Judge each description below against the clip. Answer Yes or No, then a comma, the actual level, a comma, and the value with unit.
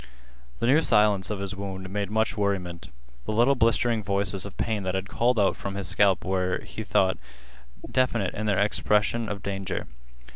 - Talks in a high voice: No, low, 100 Hz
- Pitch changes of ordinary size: No, narrow, 2.3 semitones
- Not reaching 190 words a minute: Yes, average, 180 wpm